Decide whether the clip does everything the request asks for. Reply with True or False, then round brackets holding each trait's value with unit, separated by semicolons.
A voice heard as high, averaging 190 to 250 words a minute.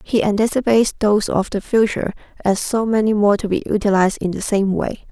True (210 Hz; 200 wpm)